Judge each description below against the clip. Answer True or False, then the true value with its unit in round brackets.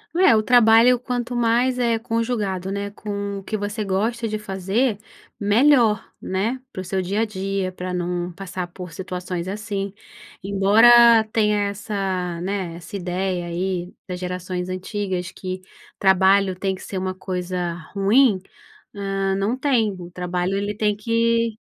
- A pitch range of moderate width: True (3.3 semitones)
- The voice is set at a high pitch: True (195 Hz)